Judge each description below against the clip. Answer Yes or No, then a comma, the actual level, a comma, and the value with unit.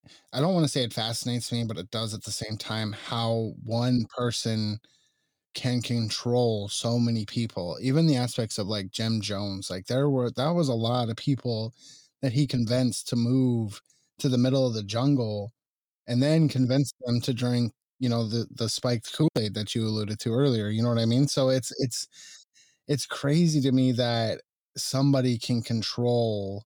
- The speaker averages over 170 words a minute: Yes, average, 185 wpm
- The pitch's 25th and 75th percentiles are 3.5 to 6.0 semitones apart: No, average, 2.7 semitones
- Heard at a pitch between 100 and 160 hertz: Yes, low, 120 Hz